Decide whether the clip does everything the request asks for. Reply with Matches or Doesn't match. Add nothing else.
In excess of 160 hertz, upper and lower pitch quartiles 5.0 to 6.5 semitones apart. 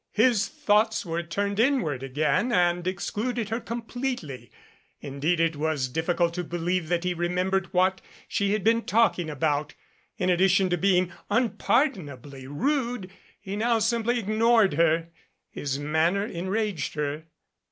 Matches